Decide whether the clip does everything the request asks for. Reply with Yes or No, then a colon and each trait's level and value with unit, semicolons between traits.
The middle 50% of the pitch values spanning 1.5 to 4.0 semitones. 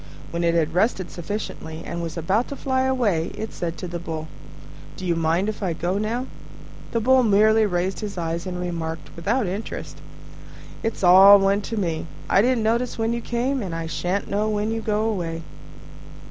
No: average, 4.6 semitones